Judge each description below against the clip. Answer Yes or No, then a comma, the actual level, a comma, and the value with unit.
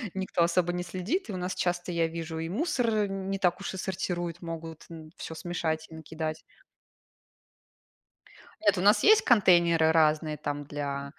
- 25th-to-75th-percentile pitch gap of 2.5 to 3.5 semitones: Yes, average, 2.9 semitones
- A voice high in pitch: No, medium, 170 Hz